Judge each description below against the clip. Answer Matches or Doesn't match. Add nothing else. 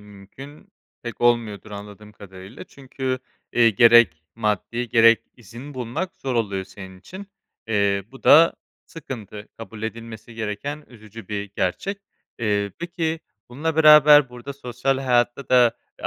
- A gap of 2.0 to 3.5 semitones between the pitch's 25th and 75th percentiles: Doesn't match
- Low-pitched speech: Matches